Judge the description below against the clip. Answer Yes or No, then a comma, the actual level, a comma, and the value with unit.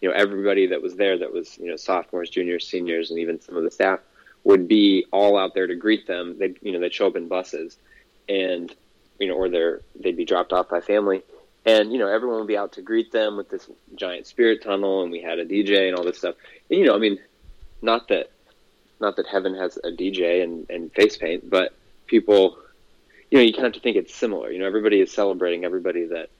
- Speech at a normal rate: No, fast, 240 wpm